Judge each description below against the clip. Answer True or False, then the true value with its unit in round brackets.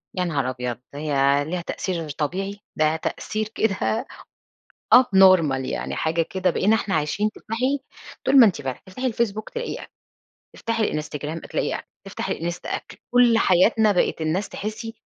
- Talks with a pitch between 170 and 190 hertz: True (185 Hz)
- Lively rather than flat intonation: True (6.0 semitones)